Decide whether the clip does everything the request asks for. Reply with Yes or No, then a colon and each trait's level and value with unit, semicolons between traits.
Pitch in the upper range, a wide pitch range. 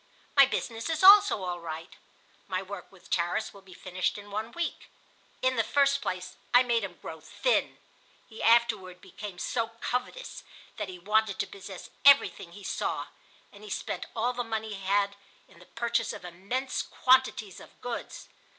No: high, 210 Hz; average, 4.8 semitones